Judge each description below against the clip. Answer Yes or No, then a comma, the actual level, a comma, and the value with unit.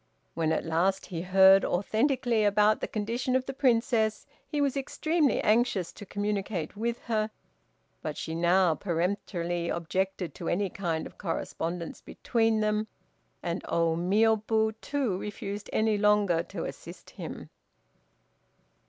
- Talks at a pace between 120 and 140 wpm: Yes, slow, 135 wpm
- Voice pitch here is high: Yes, high, 205 Hz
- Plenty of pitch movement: No, average, 4.1 semitones